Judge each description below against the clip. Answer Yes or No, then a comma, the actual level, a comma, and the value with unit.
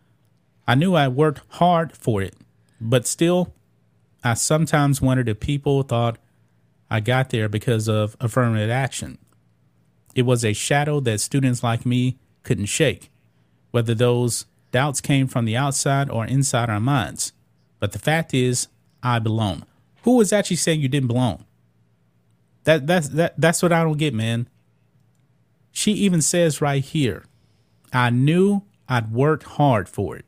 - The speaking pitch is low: Yes, low, 125 Hz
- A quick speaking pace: No, average, 155 wpm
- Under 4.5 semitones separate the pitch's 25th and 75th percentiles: No, average, 4.8 semitones